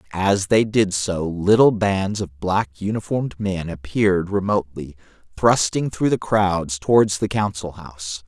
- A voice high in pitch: No, very low, 95 Hz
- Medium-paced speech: Yes, average, 150 wpm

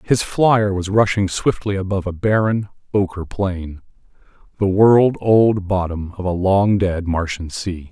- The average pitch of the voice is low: Yes, very low, 95 Hz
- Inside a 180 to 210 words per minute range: No, average, 145 wpm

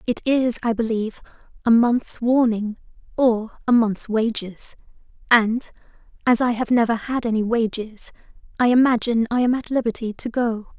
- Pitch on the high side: Yes, high, 230 Hz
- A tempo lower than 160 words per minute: Yes, average, 150 wpm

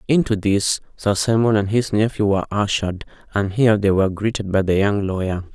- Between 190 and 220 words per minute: Yes, average, 195 wpm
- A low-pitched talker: Yes, low, 105 Hz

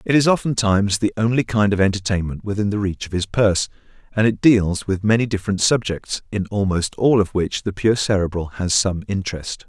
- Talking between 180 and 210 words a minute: Yes, average, 200 wpm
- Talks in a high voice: No, low, 100 Hz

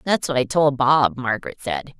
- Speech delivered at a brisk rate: Yes, fast, 210 wpm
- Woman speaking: Yes, female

